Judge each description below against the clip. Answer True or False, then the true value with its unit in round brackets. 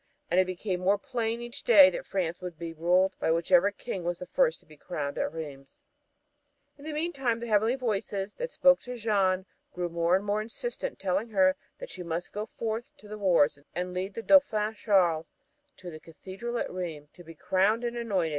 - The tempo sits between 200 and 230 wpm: True (205 wpm)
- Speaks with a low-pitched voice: False (195 Hz)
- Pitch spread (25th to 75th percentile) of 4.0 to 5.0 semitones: True (4.7 semitones)